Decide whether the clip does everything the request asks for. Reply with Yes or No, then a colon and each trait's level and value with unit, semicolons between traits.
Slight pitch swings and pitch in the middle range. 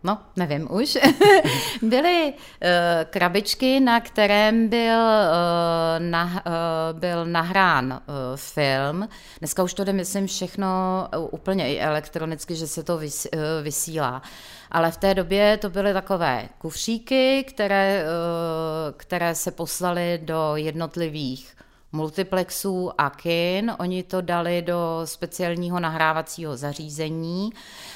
No: average, 3.5 semitones; medium, 175 Hz